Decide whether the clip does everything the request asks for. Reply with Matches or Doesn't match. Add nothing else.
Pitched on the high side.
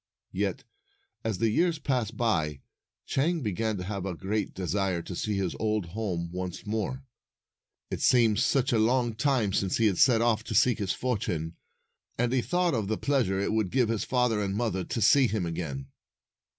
Doesn't match